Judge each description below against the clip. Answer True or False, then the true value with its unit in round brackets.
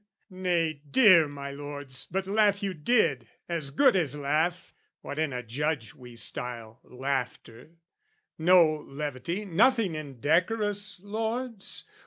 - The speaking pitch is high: False (160 Hz)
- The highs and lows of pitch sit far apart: True (5.9 semitones)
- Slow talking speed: True (120 wpm)